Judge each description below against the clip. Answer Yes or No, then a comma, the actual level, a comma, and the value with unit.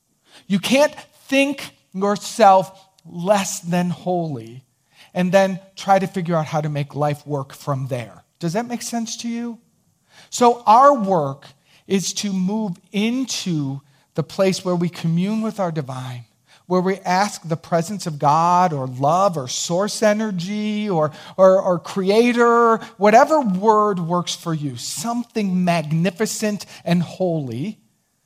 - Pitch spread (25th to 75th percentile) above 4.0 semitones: Yes, average, 5.2 semitones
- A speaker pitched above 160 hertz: Yes, medium, 185 Hz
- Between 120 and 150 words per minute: Yes, average, 140 wpm